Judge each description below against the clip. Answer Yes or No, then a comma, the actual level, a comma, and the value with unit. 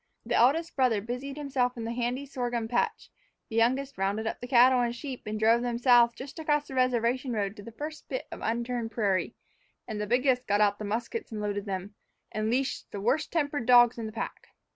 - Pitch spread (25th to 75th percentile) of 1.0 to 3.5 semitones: Yes, average, 2.9 semitones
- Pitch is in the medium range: No, high, 240 Hz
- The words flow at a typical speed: No, fast, 215 wpm